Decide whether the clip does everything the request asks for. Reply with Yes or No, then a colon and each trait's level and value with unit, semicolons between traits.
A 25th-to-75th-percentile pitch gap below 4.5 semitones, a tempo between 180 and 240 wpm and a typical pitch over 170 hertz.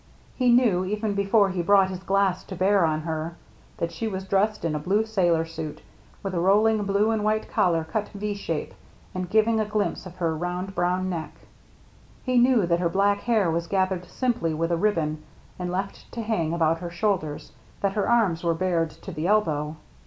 Yes: average, 3.8 semitones; average, 200 wpm; medium, 185 Hz